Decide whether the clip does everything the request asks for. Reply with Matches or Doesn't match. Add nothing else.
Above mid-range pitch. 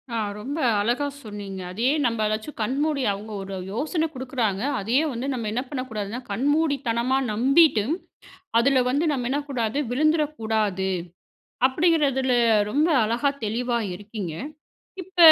Matches